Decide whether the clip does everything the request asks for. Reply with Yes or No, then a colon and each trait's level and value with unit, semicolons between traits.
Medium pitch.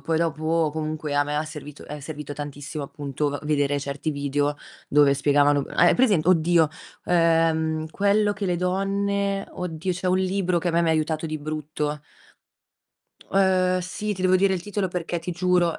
Yes: medium, 160 Hz